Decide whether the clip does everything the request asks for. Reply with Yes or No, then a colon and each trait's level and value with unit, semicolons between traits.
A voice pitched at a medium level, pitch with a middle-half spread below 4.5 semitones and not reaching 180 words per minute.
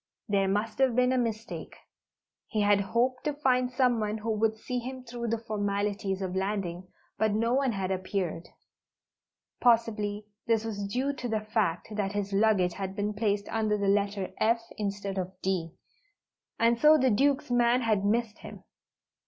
No: high, 215 Hz; average, 2.9 semitones; average, 170 wpm